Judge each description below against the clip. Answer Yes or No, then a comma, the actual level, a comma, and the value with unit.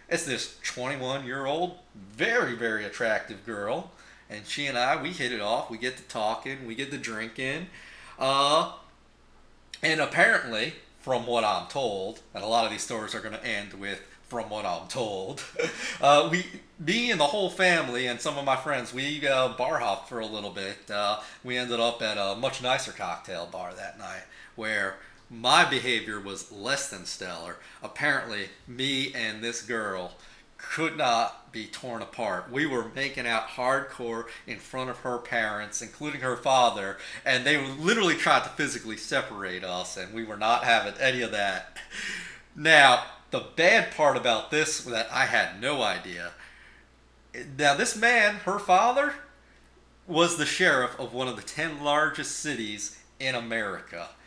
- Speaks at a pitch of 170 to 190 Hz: No, low, 125 Hz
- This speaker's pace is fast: No, average, 170 wpm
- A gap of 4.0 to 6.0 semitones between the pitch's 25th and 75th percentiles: Yes, average, 4.6 semitones